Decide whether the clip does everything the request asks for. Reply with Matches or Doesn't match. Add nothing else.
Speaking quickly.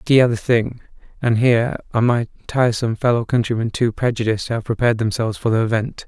Doesn't match